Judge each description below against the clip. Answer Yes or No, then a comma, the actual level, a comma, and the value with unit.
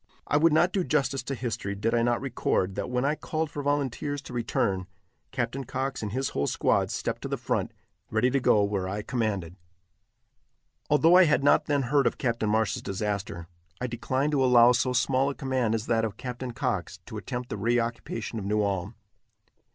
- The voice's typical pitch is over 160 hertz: No, low, 120 Hz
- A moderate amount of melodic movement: Yes, average, 4.1 semitones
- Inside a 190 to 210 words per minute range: Yes, average, 200 wpm